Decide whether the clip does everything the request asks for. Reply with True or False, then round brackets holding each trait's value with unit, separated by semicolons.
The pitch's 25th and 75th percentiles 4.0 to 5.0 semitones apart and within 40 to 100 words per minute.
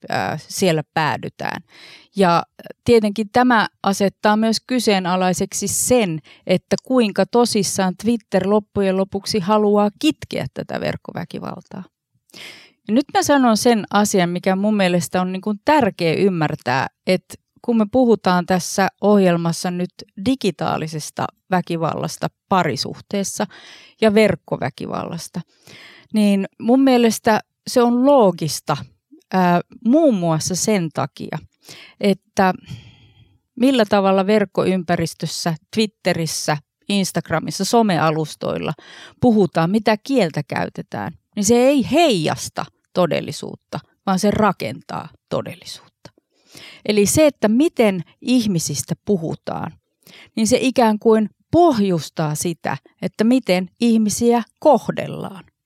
True (4.5 semitones; 95 wpm)